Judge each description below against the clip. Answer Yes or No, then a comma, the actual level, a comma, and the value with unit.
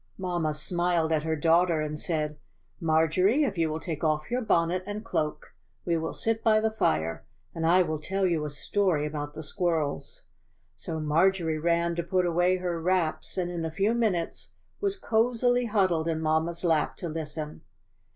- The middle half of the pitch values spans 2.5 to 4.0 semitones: Yes, average, 2.9 semitones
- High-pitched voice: No, medium, 170 Hz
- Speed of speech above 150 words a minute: Yes, average, 180 wpm